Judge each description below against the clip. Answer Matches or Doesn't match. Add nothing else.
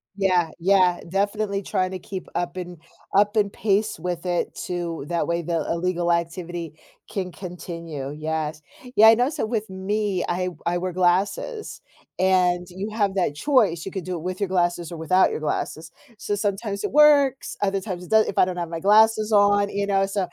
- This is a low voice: Doesn't match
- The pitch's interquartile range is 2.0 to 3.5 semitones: Matches